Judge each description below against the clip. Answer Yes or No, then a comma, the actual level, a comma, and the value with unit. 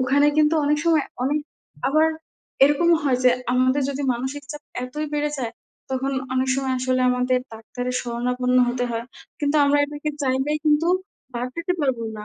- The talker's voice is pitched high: Yes, very high, 265 Hz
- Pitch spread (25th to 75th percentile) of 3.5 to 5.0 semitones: No, average, 2.8 semitones